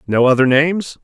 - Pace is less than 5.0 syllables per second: No, 5.8 syllables/s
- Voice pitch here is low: No, medium, 145 Hz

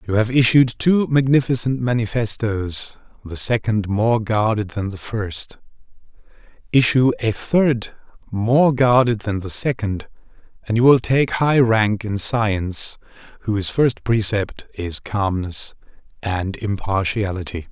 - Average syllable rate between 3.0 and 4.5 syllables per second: Yes, 4.0 syllables/s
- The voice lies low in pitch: Yes, low, 110 Hz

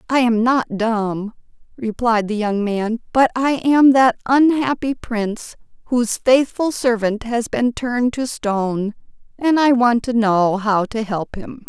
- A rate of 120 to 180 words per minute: Yes, average, 160 wpm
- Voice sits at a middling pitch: No, high, 235 Hz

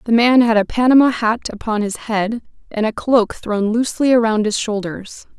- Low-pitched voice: No, high, 225 Hz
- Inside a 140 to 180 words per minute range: No, average, 190 wpm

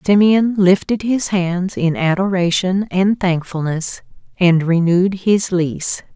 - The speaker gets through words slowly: Yes, slow, 115 wpm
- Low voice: No, medium, 185 Hz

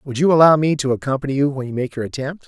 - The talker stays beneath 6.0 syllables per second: No, 7.0 syllables/s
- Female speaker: No, male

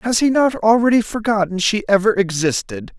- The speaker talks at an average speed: Yes, average, 160 wpm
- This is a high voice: Yes, high, 205 Hz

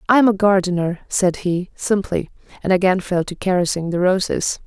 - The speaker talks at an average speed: Yes, average, 180 wpm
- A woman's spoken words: Yes, female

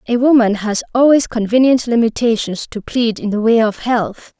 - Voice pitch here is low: No, high, 230 Hz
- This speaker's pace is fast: No, average, 180 wpm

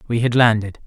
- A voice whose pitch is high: No, low, 115 Hz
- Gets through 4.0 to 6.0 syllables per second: Yes, 5.9 syllables/s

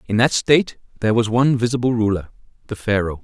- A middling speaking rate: Yes, average, 165 wpm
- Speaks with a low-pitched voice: Yes, low, 115 Hz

